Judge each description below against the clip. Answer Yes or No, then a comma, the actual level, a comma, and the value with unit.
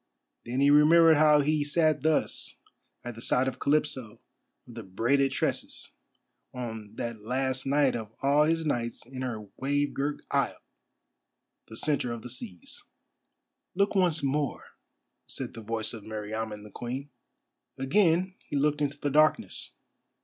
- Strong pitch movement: No, average, 4.3 semitones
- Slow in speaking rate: No, average, 150 wpm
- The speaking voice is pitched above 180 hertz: No, low, 135 Hz